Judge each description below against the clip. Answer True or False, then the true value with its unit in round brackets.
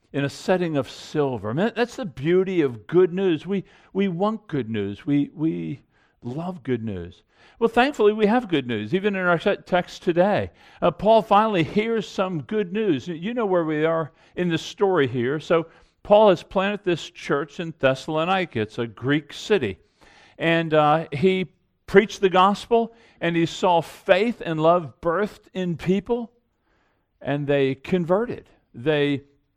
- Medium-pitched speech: True (175 Hz)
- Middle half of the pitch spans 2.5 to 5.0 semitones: False (5.5 semitones)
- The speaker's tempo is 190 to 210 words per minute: False (165 wpm)